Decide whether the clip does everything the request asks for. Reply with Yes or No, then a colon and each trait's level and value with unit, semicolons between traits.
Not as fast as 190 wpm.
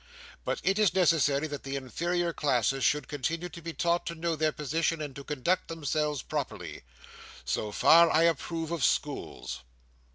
Yes: average, 165 wpm